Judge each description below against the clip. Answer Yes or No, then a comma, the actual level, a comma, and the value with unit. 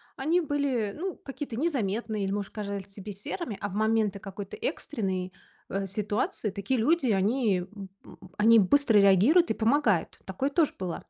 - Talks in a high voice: Yes, high, 215 Hz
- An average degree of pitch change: No, wide, 5.7 semitones